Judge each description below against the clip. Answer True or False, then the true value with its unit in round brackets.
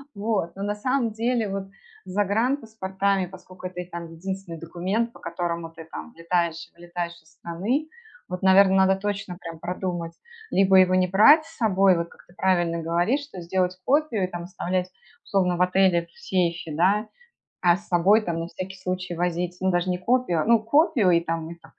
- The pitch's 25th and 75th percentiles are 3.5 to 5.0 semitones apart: False (2.8 semitones)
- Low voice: False (185 Hz)